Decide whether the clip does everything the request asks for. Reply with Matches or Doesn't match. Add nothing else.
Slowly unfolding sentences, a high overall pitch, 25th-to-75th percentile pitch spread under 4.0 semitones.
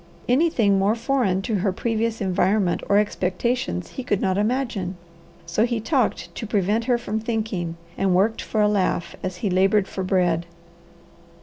Doesn't match